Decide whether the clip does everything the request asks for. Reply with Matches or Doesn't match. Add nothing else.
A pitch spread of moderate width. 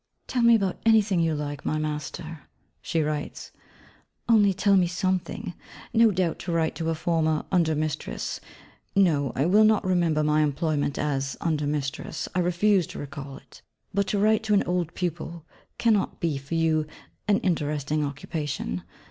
Matches